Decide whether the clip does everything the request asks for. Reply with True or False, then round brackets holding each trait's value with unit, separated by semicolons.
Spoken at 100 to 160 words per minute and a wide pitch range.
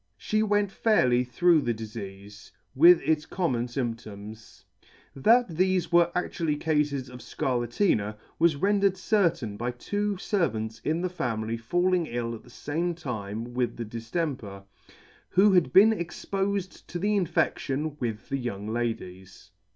True (145 wpm; 7.6 semitones)